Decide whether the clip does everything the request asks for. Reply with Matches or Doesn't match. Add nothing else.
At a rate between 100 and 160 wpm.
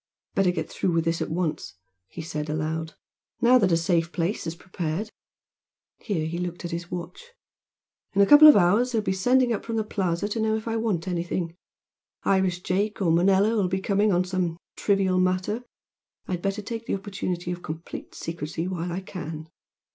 Doesn't match